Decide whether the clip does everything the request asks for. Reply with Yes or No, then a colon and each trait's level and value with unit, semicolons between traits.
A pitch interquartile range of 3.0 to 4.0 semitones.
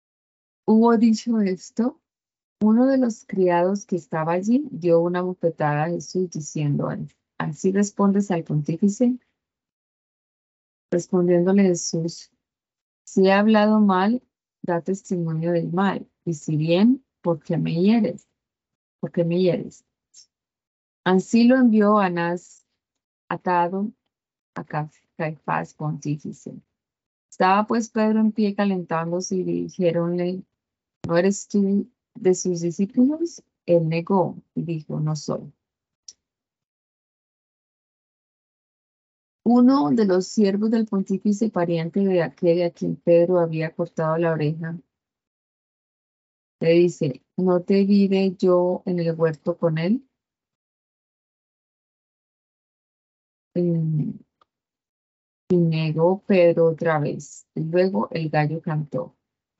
Yes: average, 3.6 semitones